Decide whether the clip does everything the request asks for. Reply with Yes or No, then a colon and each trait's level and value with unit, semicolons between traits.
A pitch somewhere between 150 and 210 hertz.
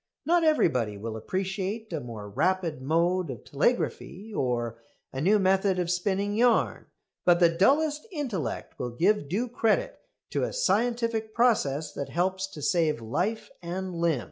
Yes: medium, 185 Hz